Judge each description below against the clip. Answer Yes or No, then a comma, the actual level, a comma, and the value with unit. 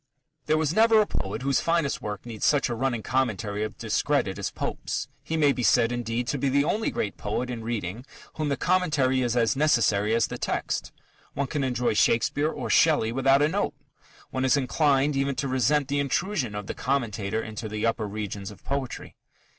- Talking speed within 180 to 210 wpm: Yes, average, 200 wpm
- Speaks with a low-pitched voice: Yes, low, 130 Hz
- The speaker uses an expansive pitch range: No, average, 4.2 semitones